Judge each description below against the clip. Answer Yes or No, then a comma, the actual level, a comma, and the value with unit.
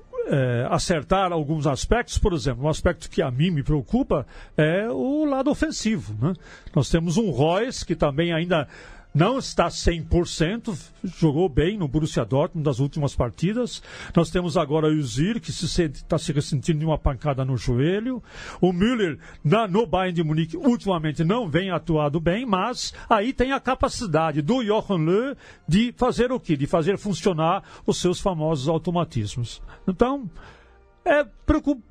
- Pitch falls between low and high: Yes, medium, 175 Hz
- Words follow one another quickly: No, average, 160 wpm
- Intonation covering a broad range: Yes, wide, 5.7 semitones